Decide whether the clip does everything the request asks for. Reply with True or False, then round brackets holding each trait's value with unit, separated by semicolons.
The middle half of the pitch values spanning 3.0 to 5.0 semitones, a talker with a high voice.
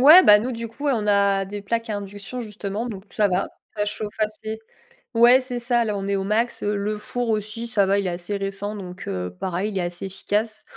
False (2.6 semitones; 210 Hz)